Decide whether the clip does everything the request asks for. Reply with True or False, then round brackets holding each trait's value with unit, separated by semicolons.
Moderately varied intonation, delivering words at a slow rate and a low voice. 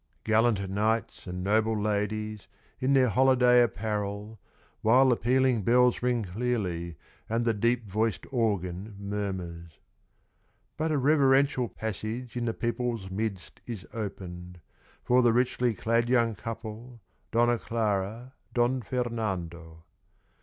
True (3.4 semitones; 120 wpm; 110 Hz)